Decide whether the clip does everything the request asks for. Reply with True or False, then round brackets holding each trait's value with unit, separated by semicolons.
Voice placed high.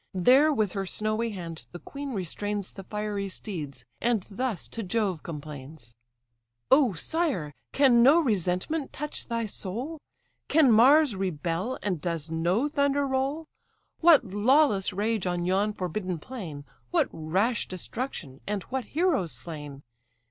True (205 Hz)